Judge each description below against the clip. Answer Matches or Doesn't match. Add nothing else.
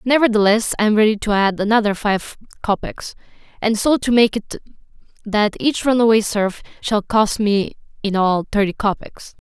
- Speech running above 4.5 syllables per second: Matches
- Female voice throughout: Matches